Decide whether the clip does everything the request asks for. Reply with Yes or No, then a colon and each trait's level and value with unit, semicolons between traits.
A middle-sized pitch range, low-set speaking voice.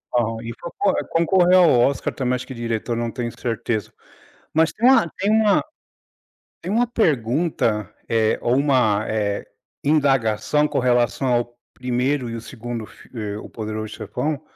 Yes: average, 4.9 semitones; low, 125 Hz